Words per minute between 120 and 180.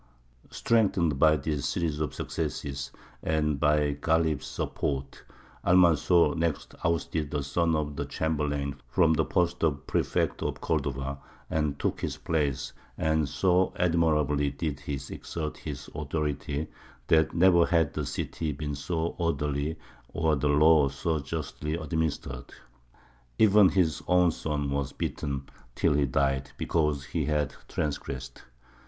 Yes: slow, 135 wpm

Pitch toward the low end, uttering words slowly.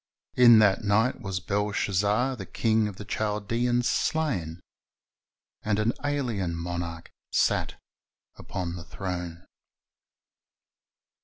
Yes: low, 105 Hz; slow, 105 wpm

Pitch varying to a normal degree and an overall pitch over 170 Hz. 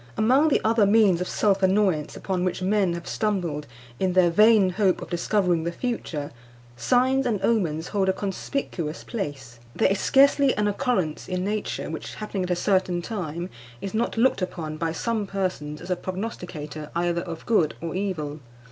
Yes: average, 3.9 semitones; medium, 185 Hz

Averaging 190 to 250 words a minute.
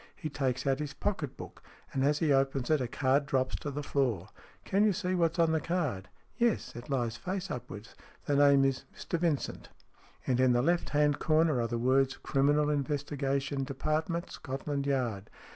Yes: average, 195 wpm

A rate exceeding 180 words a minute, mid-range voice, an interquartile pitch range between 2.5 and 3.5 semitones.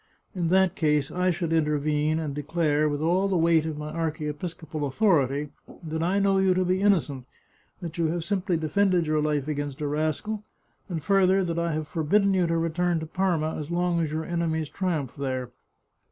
Yes: average, 195 wpm; medium, 165 Hz; average, 3.1 semitones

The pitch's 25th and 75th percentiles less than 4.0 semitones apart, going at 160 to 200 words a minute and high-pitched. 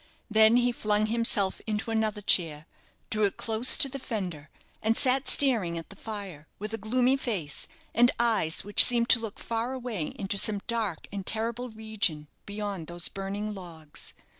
Yes: average, 3.2 semitones; average, 170 wpm; high, 215 Hz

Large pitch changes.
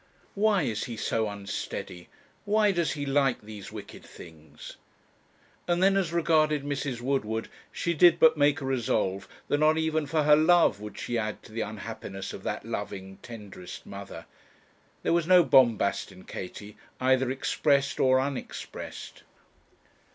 Yes: wide, 6.7 semitones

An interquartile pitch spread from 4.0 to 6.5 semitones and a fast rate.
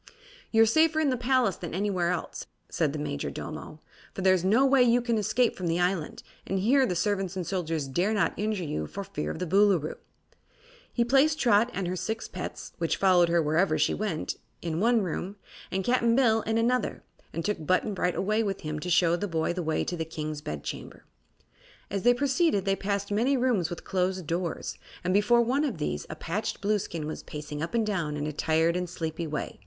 Yes: average, 5.2 semitones; fast, 210 wpm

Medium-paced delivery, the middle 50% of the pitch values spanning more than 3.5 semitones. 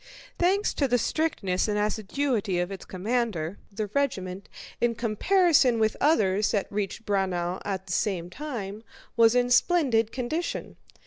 Yes: average, 145 wpm; average, 4.6 semitones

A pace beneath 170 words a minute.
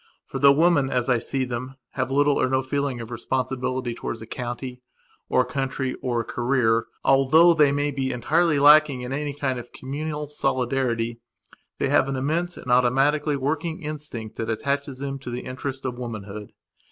No: average, 175 wpm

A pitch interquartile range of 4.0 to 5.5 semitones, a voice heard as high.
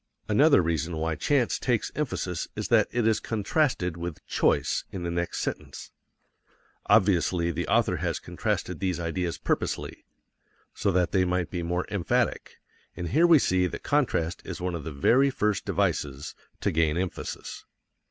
No: average, 4.3 semitones; very low, 90 Hz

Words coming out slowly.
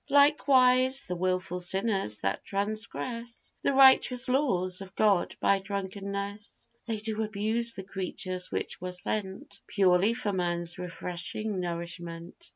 Yes: slow, 125 wpm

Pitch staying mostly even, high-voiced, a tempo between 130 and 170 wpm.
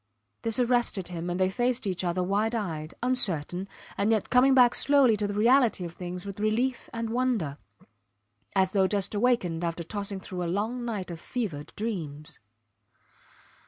No: average, 5.0 semitones; high, 200 Hz; average, 165 wpm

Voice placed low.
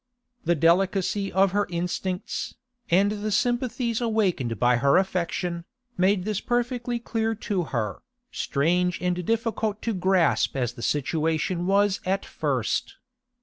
No: high, 190 Hz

